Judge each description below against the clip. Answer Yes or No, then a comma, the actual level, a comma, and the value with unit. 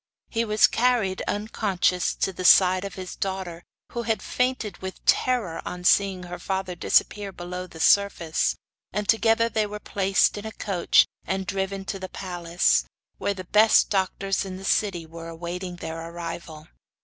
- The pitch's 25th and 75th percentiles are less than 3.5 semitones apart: Yes, average, 2.7 semitones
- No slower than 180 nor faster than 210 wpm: No, average, 165 wpm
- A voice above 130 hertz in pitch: Yes, high, 190 Hz